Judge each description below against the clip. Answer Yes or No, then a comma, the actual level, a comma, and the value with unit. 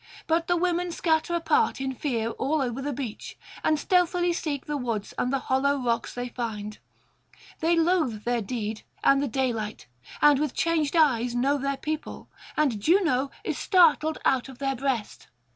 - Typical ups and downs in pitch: Yes, average, 4.8 semitones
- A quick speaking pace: No, average, 170 wpm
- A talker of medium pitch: No, very high, 275 Hz